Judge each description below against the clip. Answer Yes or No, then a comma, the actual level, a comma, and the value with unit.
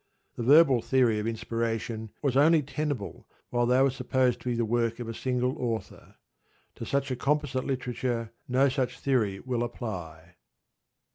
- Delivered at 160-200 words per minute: Yes, average, 165 wpm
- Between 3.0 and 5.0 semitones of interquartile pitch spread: No, narrow, 2.5 semitones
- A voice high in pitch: No, low, 125 Hz